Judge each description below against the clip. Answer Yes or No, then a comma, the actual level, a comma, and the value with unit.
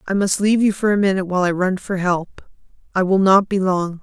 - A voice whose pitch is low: No, high, 190 Hz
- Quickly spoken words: Yes, fast, 240 wpm